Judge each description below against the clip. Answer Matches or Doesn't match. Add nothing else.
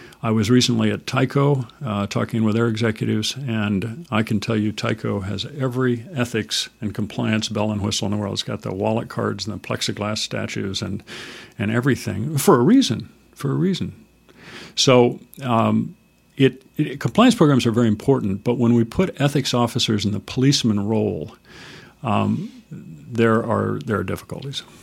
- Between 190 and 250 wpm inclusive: Doesn't match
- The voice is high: Doesn't match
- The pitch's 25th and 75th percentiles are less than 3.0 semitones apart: Doesn't match